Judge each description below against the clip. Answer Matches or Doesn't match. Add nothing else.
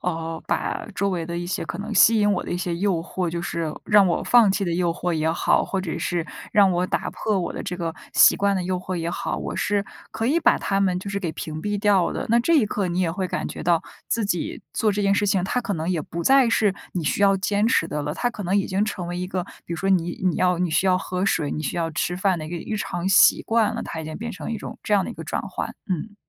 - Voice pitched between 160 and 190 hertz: Matches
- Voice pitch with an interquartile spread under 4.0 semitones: Matches